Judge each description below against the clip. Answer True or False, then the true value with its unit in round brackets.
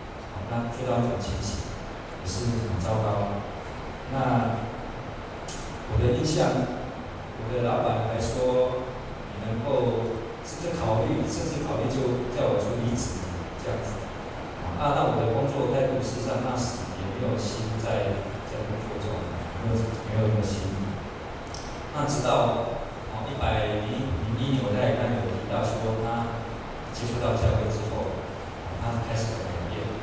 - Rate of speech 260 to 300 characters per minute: False (195 characters per minute)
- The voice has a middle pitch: False (115 Hz)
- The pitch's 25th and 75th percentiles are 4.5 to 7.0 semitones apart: False (2.6 semitones)